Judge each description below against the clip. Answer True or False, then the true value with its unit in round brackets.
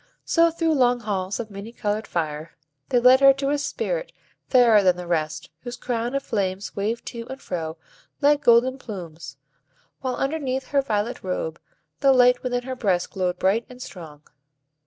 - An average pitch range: False (5.9 semitones)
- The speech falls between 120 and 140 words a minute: False (175 wpm)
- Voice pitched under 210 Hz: False (235 Hz)